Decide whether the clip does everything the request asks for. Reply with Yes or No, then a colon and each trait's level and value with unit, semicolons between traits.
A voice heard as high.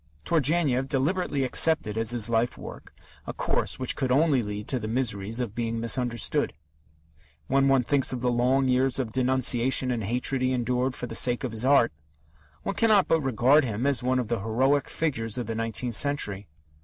No: low, 125 Hz